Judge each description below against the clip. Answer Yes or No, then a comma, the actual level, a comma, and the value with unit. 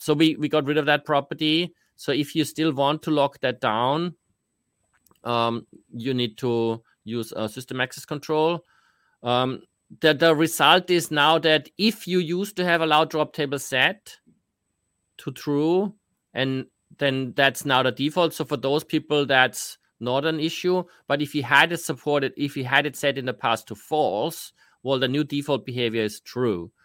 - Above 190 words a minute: No, average, 185 wpm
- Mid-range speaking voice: Yes, medium, 145 Hz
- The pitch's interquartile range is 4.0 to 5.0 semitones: No, average, 3.6 semitones